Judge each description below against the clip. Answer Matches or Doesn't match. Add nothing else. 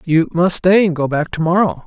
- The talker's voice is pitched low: Doesn't match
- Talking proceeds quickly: Matches